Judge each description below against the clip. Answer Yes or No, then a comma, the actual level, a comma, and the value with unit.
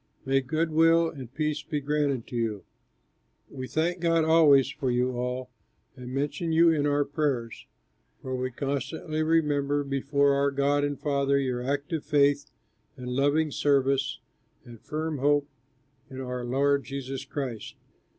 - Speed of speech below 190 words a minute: Yes, average, 150 wpm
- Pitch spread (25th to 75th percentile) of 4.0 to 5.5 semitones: No, narrow, 2.4 semitones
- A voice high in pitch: No, medium, 140 Hz